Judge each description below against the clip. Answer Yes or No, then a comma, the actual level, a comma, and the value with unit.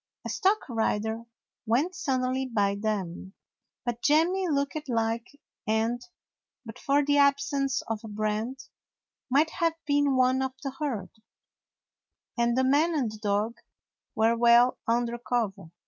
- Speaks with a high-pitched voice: Yes, high, 245 Hz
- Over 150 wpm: No, average, 140 wpm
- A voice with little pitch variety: No, average, 4.1 semitones